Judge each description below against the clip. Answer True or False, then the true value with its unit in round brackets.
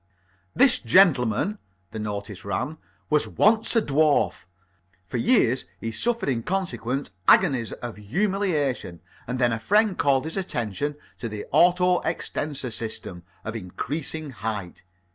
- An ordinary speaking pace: False (130 wpm)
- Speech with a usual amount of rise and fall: False (8.2 semitones)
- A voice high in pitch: False (135 Hz)